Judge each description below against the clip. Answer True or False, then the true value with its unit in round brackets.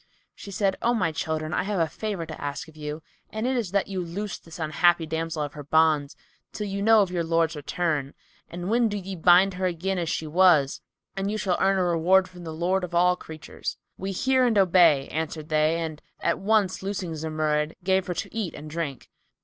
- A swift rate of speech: True (215 wpm)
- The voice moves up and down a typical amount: True (3.5 semitones)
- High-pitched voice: False (175 Hz)